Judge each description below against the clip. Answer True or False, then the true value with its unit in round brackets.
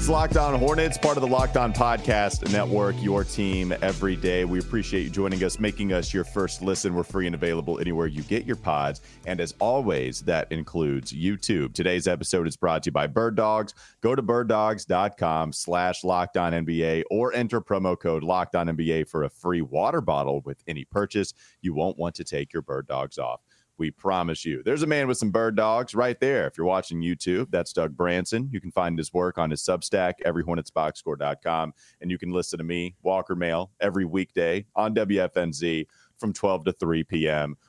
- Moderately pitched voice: False (90 Hz)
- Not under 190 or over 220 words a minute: True (200 wpm)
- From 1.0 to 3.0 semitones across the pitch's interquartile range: False (3.7 semitones)